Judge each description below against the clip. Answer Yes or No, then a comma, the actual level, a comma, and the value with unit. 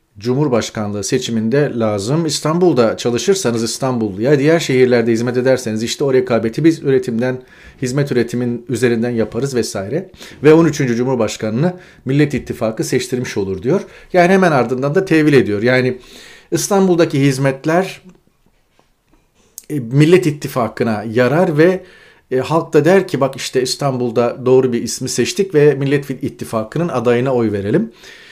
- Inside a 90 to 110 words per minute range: No, average, 125 wpm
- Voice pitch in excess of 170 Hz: No, low, 130 Hz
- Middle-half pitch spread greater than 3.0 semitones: Yes, average, 4.5 semitones